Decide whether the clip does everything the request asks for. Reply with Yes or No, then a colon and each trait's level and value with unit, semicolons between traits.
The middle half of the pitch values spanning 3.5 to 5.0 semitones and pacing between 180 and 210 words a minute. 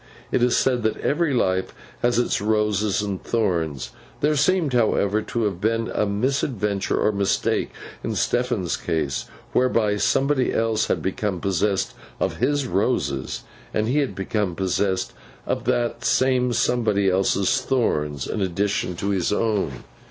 No: average, 4.4 semitones; average, 145 wpm